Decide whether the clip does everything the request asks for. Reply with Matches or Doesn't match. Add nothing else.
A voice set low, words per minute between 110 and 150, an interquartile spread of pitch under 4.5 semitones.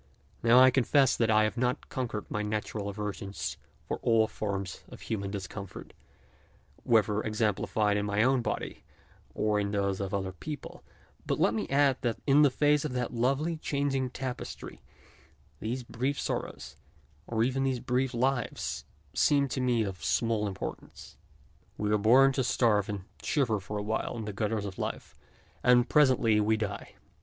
Doesn't match